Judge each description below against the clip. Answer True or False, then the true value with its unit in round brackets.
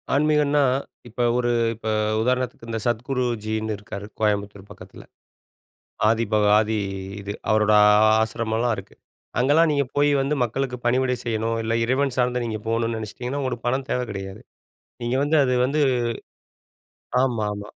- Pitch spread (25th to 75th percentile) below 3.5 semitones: True (3.0 semitones)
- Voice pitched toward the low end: True (120 Hz)